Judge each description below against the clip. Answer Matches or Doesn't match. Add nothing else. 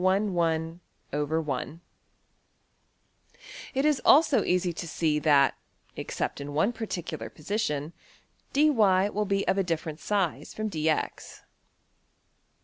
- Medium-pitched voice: Matches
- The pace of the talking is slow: Matches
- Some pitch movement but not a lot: Matches